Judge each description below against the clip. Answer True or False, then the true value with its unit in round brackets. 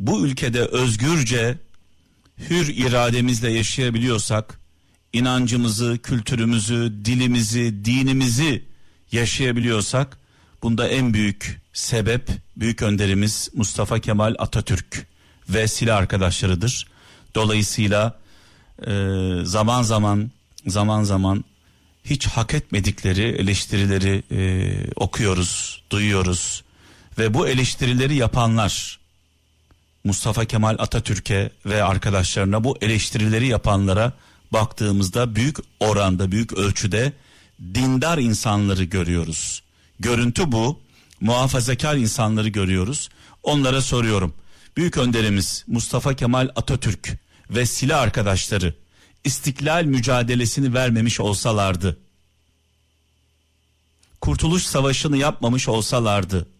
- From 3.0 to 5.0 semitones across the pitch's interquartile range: True (4.4 semitones)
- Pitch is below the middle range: True (110 Hz)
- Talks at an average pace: False (80 wpm)